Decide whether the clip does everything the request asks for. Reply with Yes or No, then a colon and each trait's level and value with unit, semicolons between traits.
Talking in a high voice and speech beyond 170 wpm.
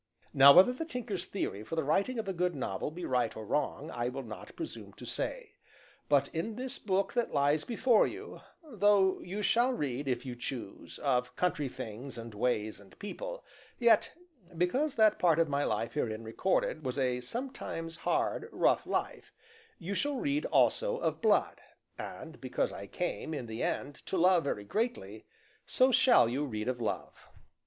No: medium, 165 Hz; average, 180 wpm